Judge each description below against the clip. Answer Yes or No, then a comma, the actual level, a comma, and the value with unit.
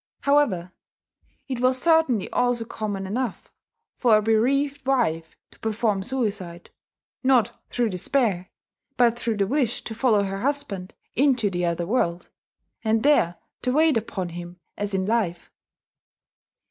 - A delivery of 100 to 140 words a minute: Yes, slow, 135 wpm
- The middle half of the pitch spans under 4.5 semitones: No, average, 5.1 semitones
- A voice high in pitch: Yes, high, 225 Hz